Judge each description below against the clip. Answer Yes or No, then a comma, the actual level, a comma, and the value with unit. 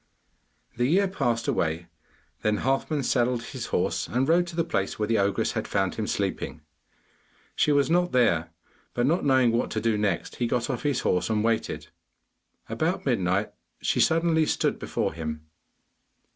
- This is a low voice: Yes, low, 120 Hz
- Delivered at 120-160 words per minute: No, average, 170 wpm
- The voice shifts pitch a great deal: Yes, wide, 5.8 semitones